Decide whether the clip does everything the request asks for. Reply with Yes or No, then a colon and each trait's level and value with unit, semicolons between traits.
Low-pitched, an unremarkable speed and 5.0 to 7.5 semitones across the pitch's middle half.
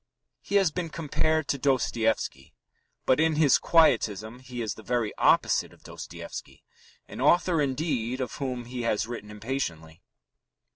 Yes: low, 125 Hz; average, 145 wpm; wide, 5.4 semitones